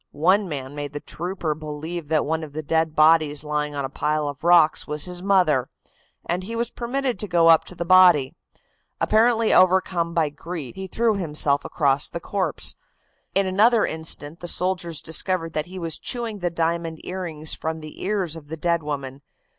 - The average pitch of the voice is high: No, medium, 165 Hz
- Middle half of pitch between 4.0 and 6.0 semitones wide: No, average, 3.6 semitones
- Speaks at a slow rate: No, average, 185 wpm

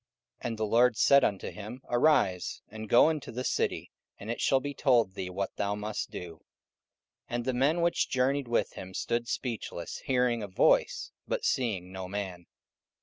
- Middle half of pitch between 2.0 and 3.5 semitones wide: No, average, 4.4 semitones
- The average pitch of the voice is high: No, low, 115 Hz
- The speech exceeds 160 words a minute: Yes, average, 180 wpm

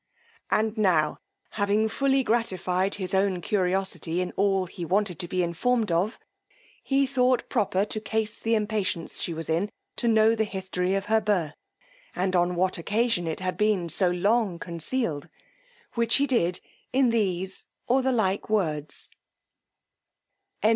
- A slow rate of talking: No, average, 155 wpm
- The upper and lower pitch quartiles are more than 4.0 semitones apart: No, average, 3.7 semitones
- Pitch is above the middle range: Yes, high, 195 Hz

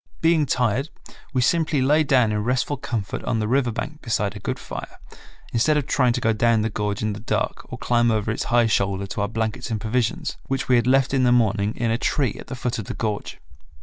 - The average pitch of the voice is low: Yes, low, 120 Hz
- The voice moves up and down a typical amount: Yes, average, 3.4 semitones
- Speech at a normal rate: No, fast, 240 wpm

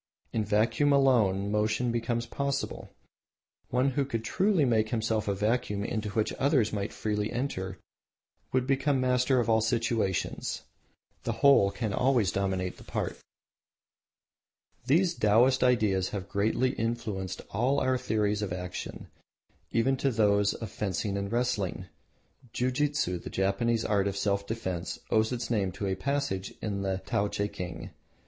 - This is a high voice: No, low, 110 Hz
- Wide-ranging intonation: No, average, 4.0 semitones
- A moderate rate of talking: Yes, average, 145 wpm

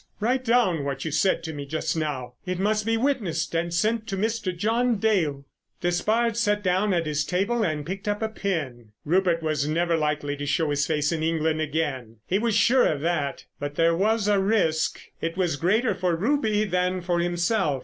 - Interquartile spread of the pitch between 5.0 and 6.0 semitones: Yes, average, 5.3 semitones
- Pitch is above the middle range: No, medium, 175 Hz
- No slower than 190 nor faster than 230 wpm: Yes, average, 200 wpm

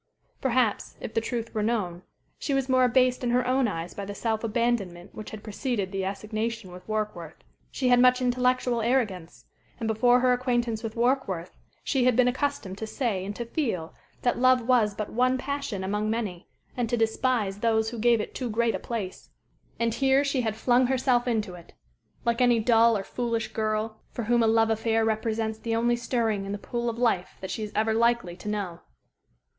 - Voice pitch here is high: Yes, high, 230 Hz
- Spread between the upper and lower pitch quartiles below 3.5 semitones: Yes, average, 2.7 semitones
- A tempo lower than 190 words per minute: No, average, 200 wpm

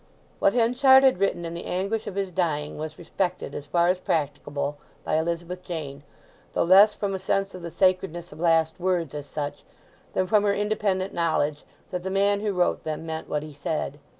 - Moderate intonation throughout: Yes, average, 3.8 semitones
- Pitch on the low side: No, medium, 175 Hz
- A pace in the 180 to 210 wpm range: Yes, average, 200 wpm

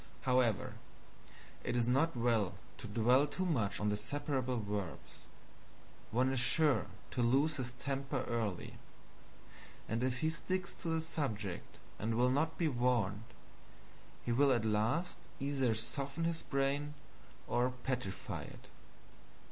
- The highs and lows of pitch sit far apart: No, average, 4.1 semitones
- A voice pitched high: No, low, 125 Hz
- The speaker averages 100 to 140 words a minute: Yes, slow, 135 wpm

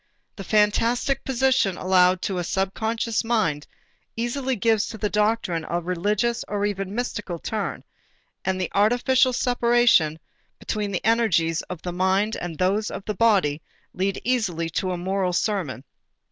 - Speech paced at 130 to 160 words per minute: Yes, average, 150 wpm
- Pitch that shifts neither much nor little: Yes, average, 4.0 semitones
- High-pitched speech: Yes, high, 200 Hz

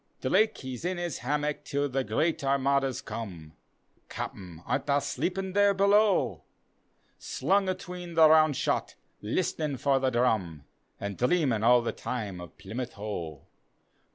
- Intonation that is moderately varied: No, wide, 7.3 semitones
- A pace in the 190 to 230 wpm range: No, average, 140 wpm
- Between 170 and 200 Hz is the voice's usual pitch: No, low, 135 Hz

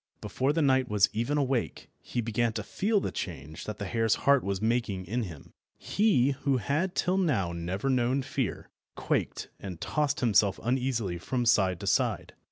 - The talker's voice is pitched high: No, low, 120 Hz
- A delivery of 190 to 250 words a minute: No, average, 175 wpm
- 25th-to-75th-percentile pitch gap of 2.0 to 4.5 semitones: No, wide, 5.4 semitones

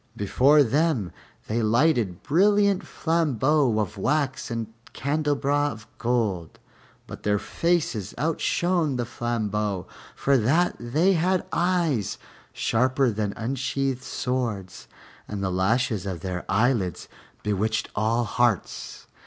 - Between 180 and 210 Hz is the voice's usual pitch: No, low, 120 Hz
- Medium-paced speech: No, slow, 110 wpm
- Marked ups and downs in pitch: Yes, wide, 5.9 semitones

